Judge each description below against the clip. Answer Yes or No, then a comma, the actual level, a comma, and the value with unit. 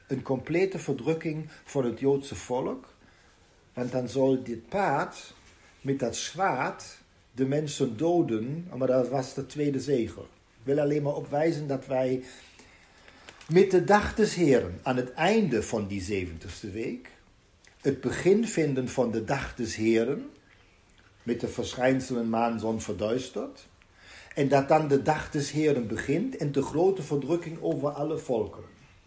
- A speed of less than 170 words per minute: Yes, average, 150 wpm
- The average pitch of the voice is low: Yes, low, 130 Hz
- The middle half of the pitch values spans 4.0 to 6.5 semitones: Yes, average, 4.9 semitones